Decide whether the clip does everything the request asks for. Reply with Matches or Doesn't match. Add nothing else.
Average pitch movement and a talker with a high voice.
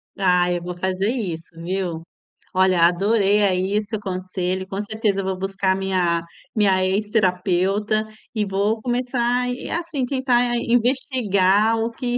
Matches